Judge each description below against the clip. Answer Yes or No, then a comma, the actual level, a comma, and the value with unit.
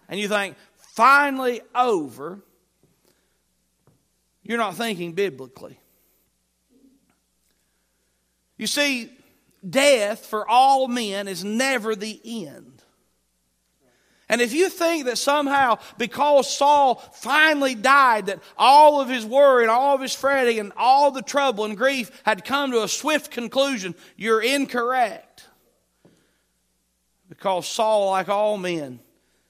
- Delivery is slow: Yes, slow, 120 wpm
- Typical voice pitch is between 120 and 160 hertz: No, high, 235 Hz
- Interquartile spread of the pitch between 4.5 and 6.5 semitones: Yes, wide, 5.4 semitones